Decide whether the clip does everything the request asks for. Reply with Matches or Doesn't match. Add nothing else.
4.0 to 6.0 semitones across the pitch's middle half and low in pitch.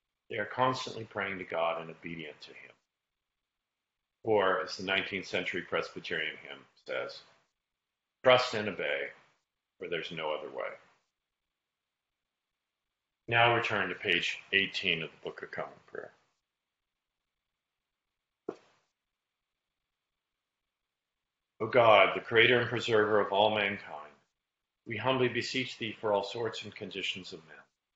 Doesn't match